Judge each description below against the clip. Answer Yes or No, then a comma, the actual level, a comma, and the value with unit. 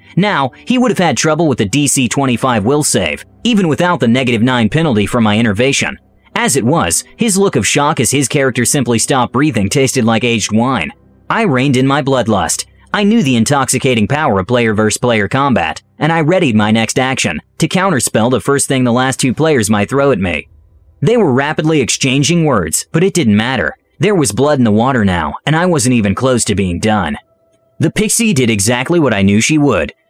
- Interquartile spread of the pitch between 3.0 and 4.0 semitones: No, average, 5.0 semitones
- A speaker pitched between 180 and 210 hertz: No, low, 130 Hz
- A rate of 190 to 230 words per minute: Yes, fast, 205 wpm